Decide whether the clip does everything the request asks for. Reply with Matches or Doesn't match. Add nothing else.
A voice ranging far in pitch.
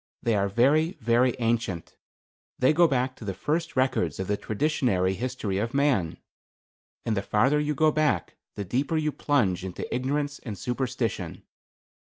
Matches